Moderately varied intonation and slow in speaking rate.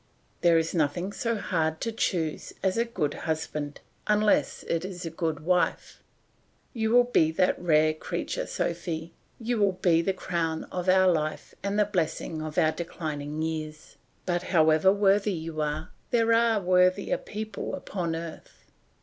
No: average, 3.9 semitones; average, 160 wpm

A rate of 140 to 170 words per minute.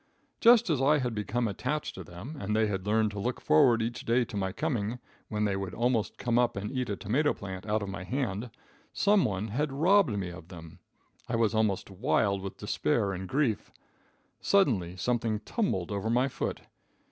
No: average, 195 wpm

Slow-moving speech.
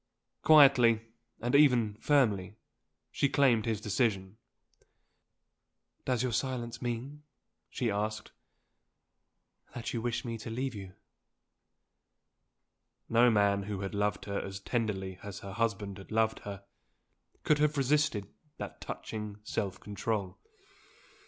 Yes: slow, 120 wpm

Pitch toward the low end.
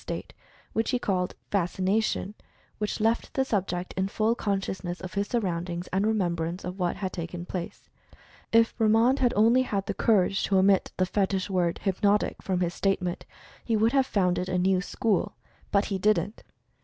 No: high, 195 Hz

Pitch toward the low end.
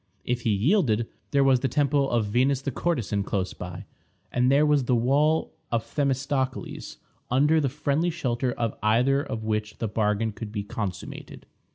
Yes: low, 125 Hz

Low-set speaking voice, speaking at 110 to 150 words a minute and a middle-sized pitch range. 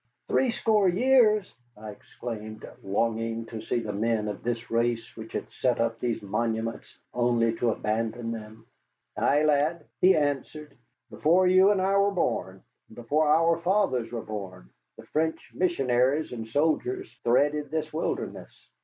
No: low, 125 Hz; average, 145 wpm; wide, 6.3 semitones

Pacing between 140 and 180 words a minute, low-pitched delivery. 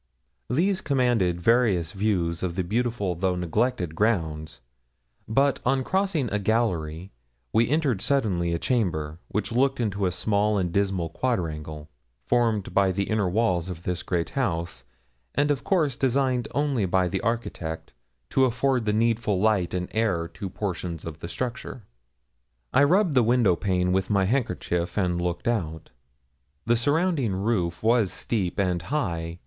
Yes: average, 155 wpm; low, 100 Hz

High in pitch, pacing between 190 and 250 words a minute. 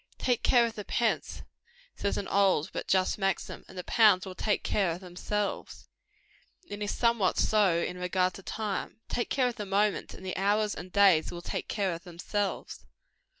Yes: high, 200 Hz; average, 195 wpm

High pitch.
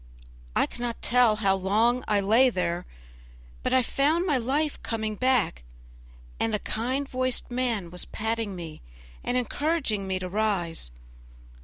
Yes: high, 225 Hz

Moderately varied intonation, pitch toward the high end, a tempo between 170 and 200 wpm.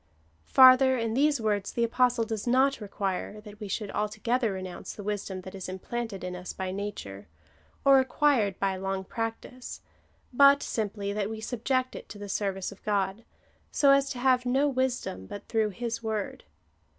Yes: average, 4.2 semitones; high, 220 Hz; average, 175 wpm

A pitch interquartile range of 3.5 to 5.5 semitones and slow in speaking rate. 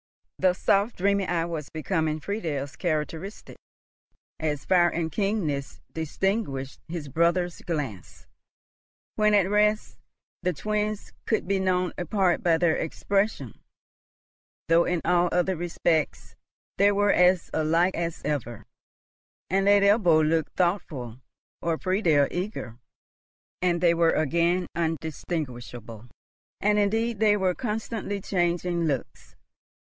Yes: average, 3.8 semitones; slow, 120 wpm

